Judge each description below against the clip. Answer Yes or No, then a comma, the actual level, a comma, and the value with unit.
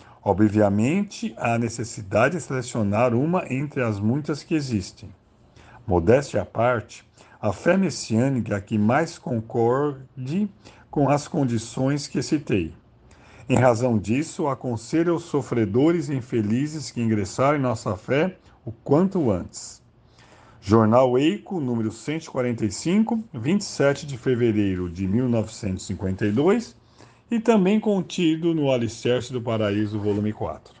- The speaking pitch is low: Yes, low, 125 Hz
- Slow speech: Yes, slow, 115 wpm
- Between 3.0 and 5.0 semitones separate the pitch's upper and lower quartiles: No, wide, 5.4 semitones